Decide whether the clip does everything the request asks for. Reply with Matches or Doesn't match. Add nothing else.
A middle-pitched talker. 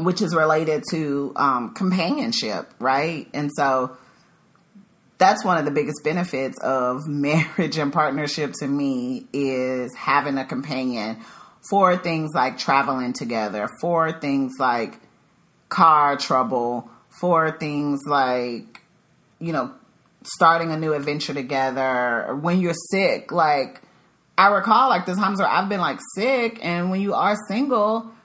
Matches